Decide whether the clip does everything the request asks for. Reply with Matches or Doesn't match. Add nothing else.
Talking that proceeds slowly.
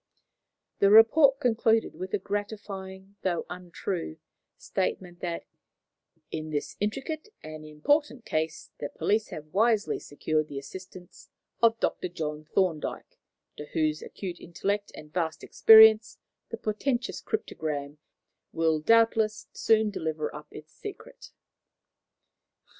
Matches